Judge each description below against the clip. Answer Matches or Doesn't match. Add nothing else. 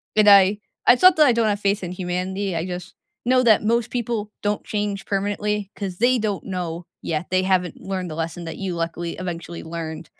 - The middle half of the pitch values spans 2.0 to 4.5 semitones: Matches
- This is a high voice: Matches